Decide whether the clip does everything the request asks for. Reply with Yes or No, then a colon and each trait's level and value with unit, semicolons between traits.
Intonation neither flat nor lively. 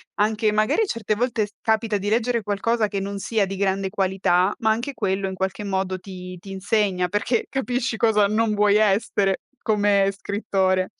No: narrow, 2.3 semitones